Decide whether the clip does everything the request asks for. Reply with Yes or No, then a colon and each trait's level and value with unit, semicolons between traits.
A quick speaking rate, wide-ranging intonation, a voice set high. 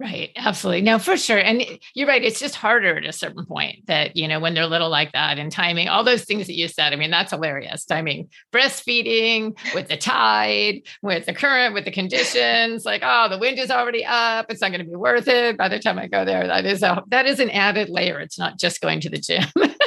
Yes: fast, 250 wpm; wide, 6.1 semitones; high, 205 Hz